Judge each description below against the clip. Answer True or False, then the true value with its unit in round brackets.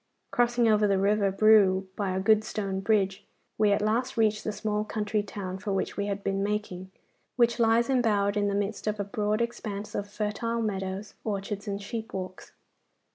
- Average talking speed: True (185 wpm)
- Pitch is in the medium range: False (210 Hz)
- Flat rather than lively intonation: True (1.6 semitones)